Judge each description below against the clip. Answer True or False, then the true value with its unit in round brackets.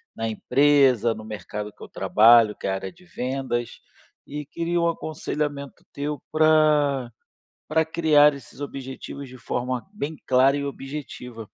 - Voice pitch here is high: False (140 Hz)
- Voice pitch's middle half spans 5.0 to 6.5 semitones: False (3.7 semitones)